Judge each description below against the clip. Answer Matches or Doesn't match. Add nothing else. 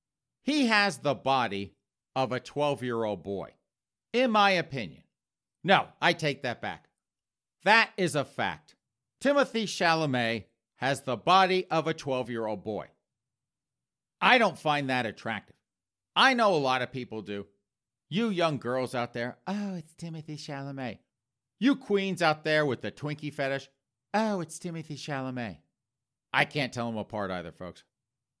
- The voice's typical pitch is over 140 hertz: Doesn't match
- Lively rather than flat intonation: Matches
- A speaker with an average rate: Matches